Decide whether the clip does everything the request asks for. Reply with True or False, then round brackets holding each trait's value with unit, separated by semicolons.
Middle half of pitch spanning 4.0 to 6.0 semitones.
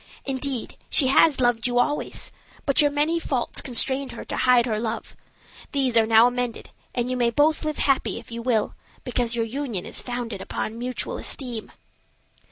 False (2.9 semitones)